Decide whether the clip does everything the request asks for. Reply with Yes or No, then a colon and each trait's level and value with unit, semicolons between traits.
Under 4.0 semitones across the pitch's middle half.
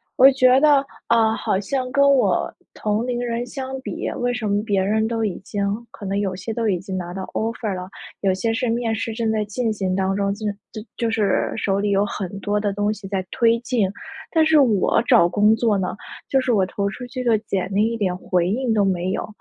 Yes: average, 3.5 semitones